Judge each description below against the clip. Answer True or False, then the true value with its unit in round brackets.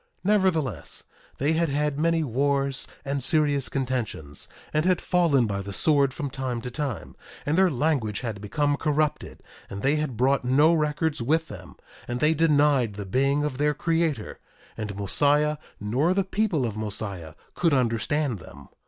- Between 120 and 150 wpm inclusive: False (160 wpm)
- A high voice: False (140 Hz)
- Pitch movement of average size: True (4.3 semitones)